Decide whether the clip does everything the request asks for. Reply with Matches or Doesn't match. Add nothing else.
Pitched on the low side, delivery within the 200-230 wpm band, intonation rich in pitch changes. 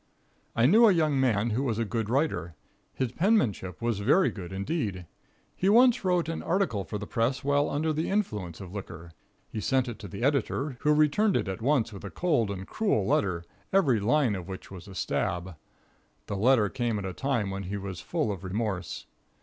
Matches